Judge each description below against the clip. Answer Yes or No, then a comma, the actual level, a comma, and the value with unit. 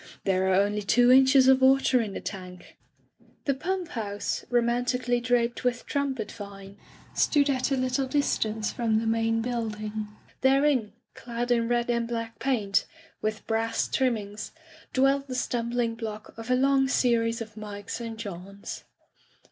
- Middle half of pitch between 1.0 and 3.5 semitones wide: Yes, average, 3.1 semitones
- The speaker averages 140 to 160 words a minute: Yes, average, 150 wpm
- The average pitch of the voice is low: No, high, 235 Hz